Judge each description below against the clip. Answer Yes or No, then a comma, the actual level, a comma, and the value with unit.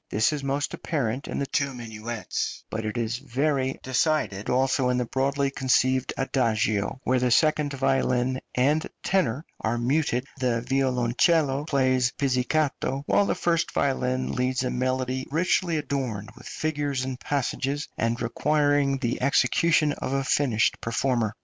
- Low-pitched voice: Yes, low, 130 Hz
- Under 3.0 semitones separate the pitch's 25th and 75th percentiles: Yes, narrow, 2.4 semitones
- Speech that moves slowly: No, average, 145 wpm